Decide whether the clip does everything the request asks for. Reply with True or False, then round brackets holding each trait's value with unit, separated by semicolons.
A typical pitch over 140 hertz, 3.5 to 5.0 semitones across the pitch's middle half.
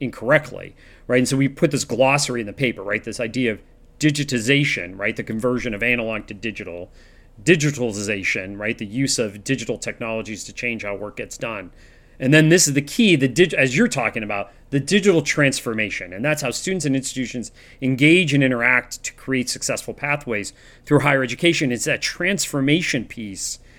False (125 Hz; 4.2 semitones)